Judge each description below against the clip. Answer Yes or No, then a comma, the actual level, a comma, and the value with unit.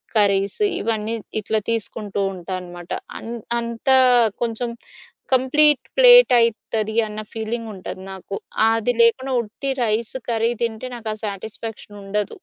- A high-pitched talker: Yes, high, 220 Hz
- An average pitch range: No, narrow, 2.2 semitones